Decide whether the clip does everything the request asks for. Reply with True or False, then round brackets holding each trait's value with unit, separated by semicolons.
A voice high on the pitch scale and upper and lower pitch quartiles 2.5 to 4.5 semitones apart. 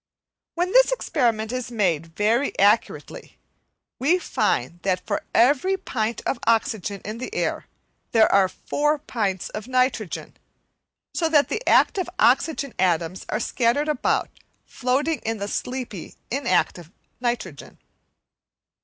False (235 Hz; 5.6 semitones)